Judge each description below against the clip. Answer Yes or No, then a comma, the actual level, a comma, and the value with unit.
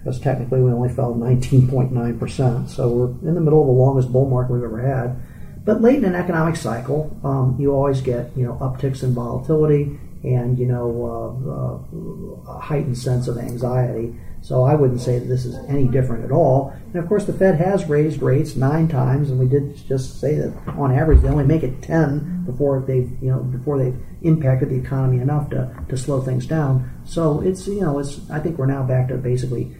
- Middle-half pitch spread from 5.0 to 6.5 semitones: No, narrow, 2.6 semitones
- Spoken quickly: Yes, fast, 215 wpm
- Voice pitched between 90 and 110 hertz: No, low, 130 Hz